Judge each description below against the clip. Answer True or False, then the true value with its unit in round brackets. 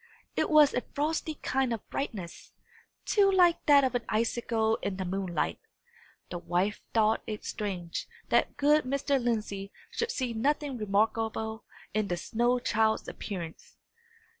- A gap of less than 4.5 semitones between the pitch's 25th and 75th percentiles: False (5.3 semitones)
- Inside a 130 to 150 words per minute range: True (140 wpm)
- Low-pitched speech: False (225 Hz)